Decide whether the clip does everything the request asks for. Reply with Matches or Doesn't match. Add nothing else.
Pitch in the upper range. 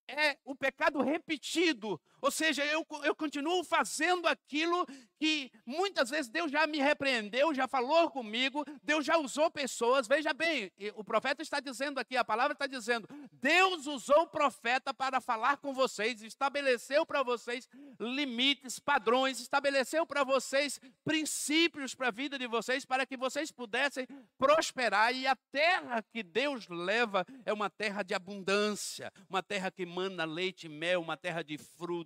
Matches